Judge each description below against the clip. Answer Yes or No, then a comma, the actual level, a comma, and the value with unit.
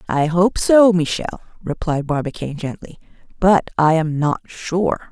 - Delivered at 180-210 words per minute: No, average, 140 wpm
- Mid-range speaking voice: Yes, medium, 170 Hz